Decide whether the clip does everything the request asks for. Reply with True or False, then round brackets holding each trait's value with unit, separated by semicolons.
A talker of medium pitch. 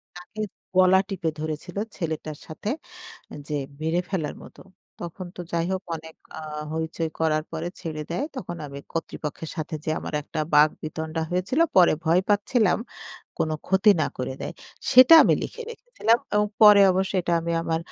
True (170 Hz)